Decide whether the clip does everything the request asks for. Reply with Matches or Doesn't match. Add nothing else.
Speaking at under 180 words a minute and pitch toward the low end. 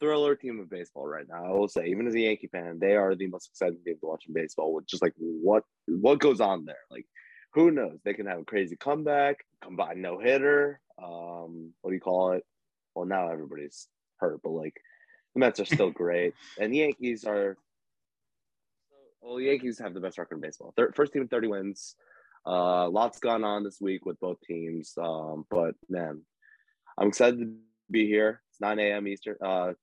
Doesn't match